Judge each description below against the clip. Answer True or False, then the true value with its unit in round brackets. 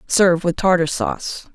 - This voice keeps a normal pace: True (155 wpm)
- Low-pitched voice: False (190 Hz)